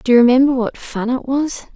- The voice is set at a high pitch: Yes, very high, 255 Hz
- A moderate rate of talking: No, fast, 240 wpm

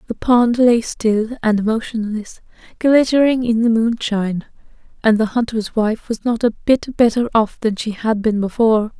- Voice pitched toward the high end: Yes, high, 225 Hz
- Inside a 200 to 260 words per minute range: No, average, 165 wpm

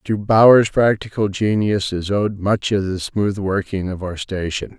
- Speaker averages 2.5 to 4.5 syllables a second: Yes, 4.3 syllables/s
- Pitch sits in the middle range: No, low, 100 Hz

